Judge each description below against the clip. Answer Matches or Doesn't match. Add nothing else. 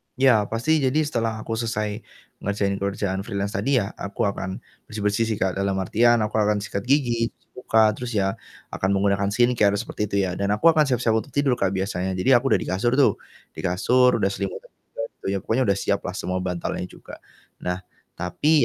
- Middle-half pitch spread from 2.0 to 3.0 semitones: Doesn't match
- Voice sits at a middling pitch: Doesn't match